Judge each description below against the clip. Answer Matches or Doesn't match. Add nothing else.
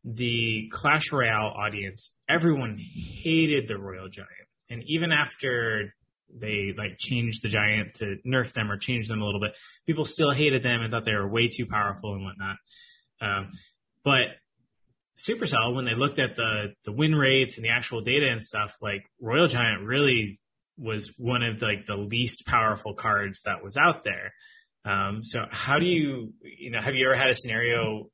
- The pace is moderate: Matches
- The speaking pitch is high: Doesn't match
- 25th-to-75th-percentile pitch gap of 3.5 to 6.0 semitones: Matches